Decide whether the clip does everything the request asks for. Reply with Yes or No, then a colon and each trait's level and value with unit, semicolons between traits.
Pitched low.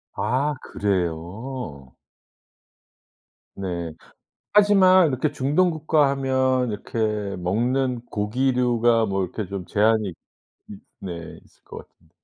Yes: low, 120 Hz